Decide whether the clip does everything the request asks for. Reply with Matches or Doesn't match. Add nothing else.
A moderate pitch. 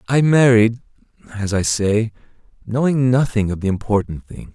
Doesn't match